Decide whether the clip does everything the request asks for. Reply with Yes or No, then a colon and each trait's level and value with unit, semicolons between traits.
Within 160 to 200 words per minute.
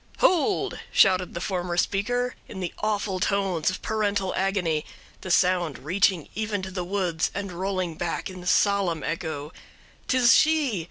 No: average, 150 wpm